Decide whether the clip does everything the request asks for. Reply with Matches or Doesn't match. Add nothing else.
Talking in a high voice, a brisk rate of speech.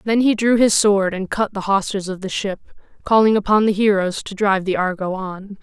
Matches